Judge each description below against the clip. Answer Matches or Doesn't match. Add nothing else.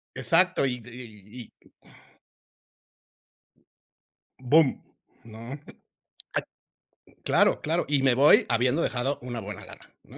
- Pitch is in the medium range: Doesn't match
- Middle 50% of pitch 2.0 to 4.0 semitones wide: Matches